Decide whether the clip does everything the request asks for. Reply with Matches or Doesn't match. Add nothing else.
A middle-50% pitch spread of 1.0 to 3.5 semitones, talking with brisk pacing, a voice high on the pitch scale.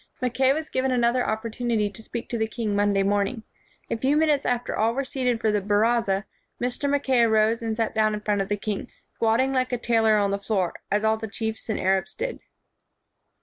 Matches